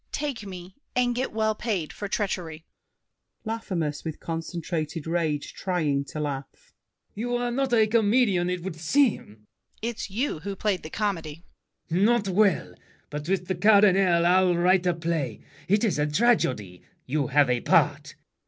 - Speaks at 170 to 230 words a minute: No, average, 160 wpm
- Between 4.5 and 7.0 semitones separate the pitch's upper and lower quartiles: Yes, average, 5.2 semitones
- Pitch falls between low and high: Yes, medium, 180 Hz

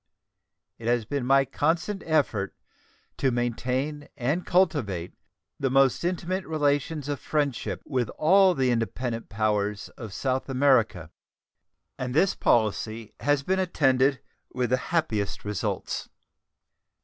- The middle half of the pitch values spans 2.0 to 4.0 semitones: No, average, 4.7 semitones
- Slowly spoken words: Yes, slow, 120 wpm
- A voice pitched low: Yes, low, 130 Hz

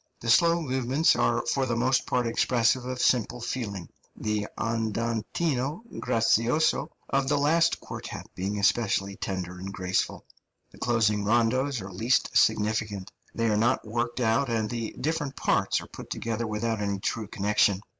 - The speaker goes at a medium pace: Yes, average, 155 wpm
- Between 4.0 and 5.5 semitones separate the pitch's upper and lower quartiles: No, average, 3.6 semitones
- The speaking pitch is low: Yes, low, 115 Hz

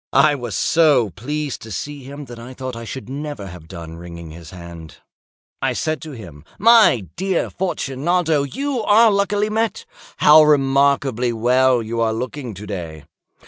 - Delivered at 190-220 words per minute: No, average, 160 wpm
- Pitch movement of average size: No, wide, 6.6 semitones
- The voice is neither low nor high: No, low, 130 Hz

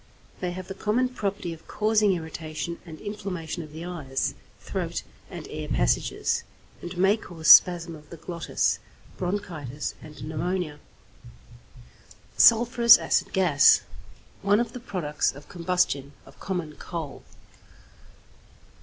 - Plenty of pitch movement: No, average, 4.3 semitones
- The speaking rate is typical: No, slow, 125 wpm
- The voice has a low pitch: No, medium, 175 Hz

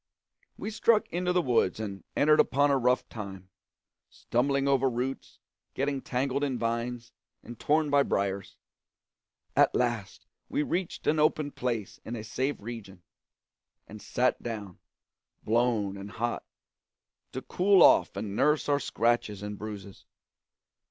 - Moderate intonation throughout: Yes, average, 5.0 semitones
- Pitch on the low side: Yes, low, 120 Hz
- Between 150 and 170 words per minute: No, average, 140 wpm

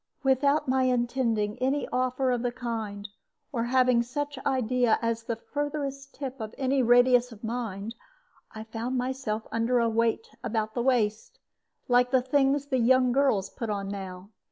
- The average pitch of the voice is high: Yes, high, 245 Hz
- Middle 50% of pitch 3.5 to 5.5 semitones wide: No, narrow, 2.6 semitones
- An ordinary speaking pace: Yes, average, 160 wpm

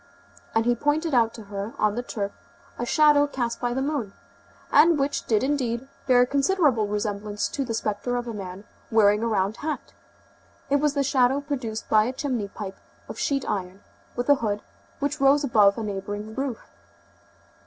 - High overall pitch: Yes, high, 240 Hz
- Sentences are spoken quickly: No, average, 180 wpm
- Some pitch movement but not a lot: Yes, average, 5.0 semitones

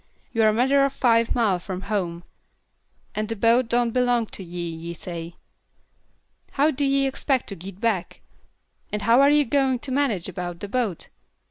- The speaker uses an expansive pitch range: Yes, wide, 5.9 semitones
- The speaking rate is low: No, average, 175 wpm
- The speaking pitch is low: No, high, 230 Hz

